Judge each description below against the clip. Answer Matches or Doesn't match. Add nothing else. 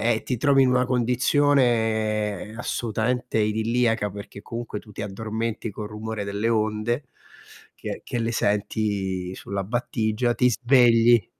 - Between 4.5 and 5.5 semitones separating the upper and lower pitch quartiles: Doesn't match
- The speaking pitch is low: Matches